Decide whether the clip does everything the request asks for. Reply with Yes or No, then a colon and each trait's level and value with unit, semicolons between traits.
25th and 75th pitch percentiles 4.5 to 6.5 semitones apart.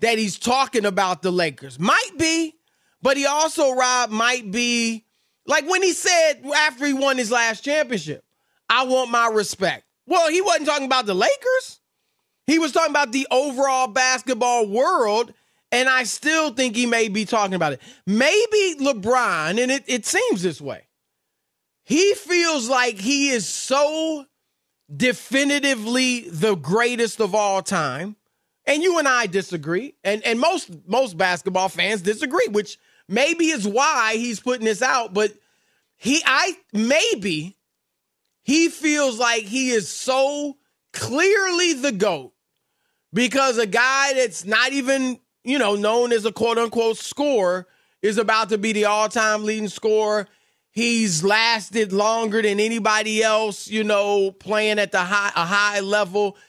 Yes: average, 4.8 semitones